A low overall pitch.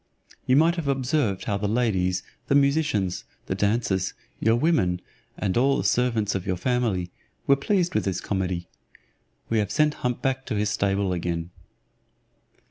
Yes: low, 110 Hz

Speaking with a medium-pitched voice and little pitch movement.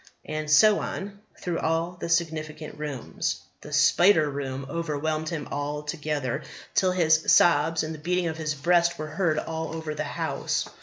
Yes: medium, 155 Hz; narrow, 1.9 semitones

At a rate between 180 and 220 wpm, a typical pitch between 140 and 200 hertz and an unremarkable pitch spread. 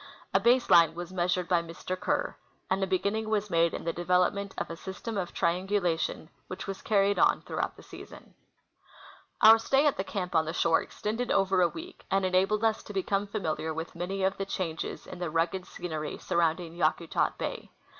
Yes: average, 200 wpm; medium, 185 Hz; average, 3.0 semitones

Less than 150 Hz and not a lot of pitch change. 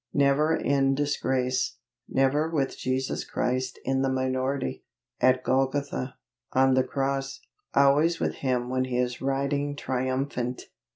Yes: low, 135 Hz; narrow, 1.4 semitones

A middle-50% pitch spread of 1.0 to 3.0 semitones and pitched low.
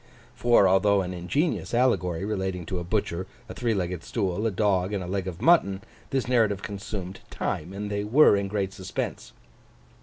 Yes: narrow, 2.5 semitones; low, 100 Hz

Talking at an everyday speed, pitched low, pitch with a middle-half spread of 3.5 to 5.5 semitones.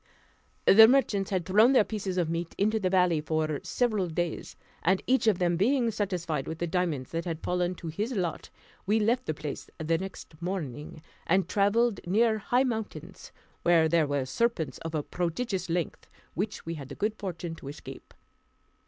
No: average, 180 wpm; medium, 180 Hz; average, 4.6 semitones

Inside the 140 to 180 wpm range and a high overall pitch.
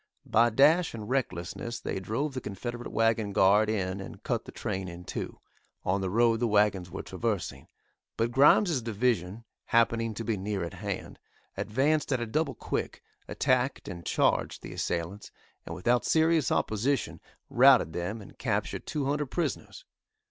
No: average, 160 wpm; low, 115 Hz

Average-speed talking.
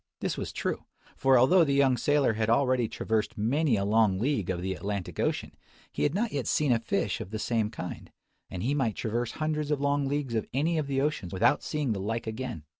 No: fast, 225 wpm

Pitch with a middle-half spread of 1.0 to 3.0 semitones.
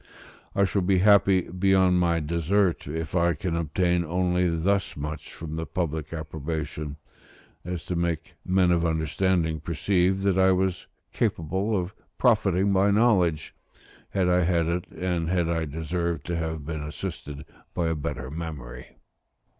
Yes: average, 2.7 semitones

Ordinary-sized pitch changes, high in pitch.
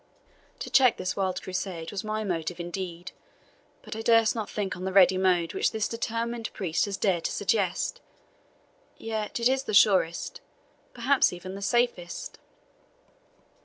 Yes: average, 3.6 semitones; high, 195 Hz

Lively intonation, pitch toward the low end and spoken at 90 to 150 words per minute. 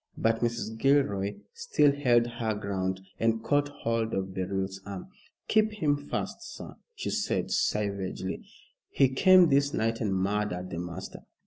Yes: wide, 6.4 semitones; low, 115 Hz; average, 145 wpm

